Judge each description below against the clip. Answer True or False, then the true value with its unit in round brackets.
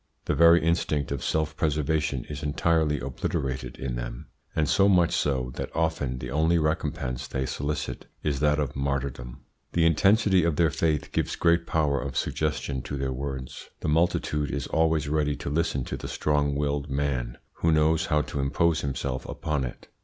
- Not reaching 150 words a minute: False (175 wpm)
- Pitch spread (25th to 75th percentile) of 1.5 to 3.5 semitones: True (2.9 semitones)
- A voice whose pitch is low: True (75 Hz)